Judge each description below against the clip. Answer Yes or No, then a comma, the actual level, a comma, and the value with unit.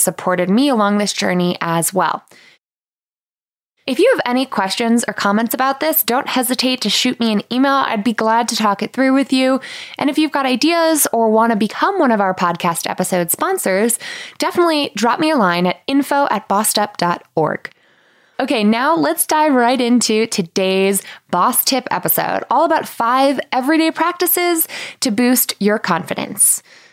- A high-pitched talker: Yes, high, 245 Hz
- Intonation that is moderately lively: No, wide, 6.1 semitones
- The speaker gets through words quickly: No, average, 165 wpm